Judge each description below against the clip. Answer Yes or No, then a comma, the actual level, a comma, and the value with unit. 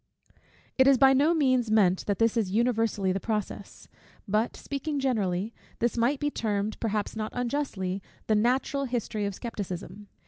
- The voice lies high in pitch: Yes, high, 225 Hz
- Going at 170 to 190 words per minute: No, average, 160 wpm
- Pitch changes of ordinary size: Yes, average, 4.1 semitones